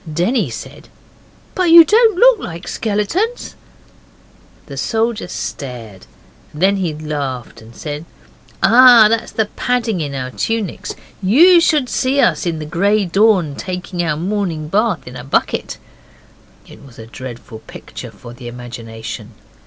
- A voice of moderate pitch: Yes, medium, 180 Hz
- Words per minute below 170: Yes, average, 140 wpm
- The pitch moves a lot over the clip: Yes, wide, 9.0 semitones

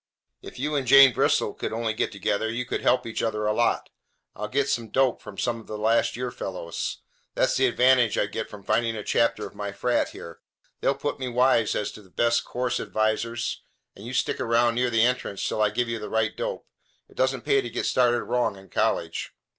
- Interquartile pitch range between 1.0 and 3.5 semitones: Yes, average, 2.7 semitones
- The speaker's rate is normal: No, fast, 225 wpm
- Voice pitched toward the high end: No, low, 115 Hz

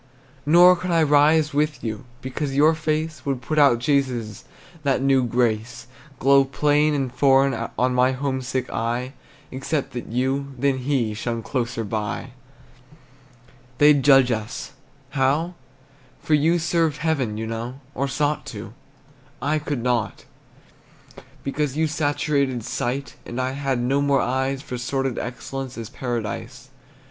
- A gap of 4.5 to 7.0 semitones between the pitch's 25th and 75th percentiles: No, average, 3.1 semitones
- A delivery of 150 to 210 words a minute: No, average, 140 wpm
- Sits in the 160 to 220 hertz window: No, low, 135 Hz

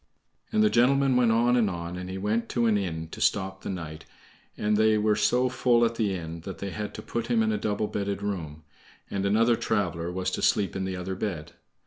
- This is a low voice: Yes, low, 105 Hz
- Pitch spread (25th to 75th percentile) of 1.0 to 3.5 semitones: No, average, 4.0 semitones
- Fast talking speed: Yes, fast, 235 wpm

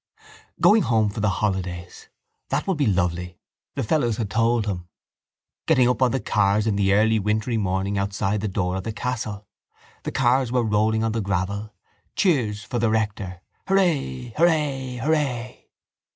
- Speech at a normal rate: Yes, average, 165 wpm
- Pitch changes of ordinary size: Yes, average, 3.9 semitones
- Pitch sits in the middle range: No, low, 110 Hz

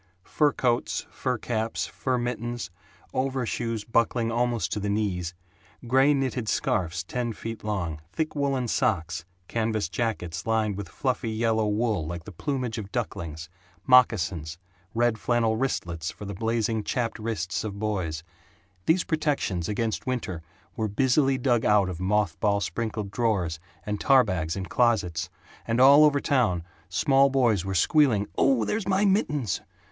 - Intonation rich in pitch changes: No, average, 4.6 semitones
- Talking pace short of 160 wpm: Yes, average, 150 wpm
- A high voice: No, low, 110 Hz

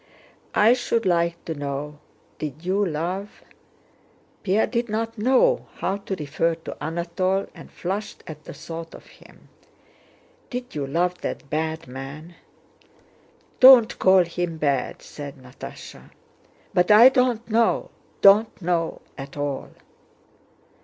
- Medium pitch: Yes, medium, 175 Hz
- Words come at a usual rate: No, slow, 125 wpm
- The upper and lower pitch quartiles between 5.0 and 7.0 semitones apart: Yes, wide, 5.5 semitones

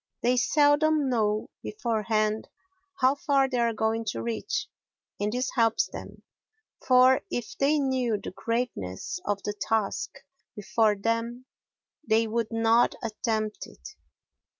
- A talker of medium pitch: No, high, 230 Hz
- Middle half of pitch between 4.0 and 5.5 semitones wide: No, average, 3.0 semitones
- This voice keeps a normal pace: No, slow, 125 wpm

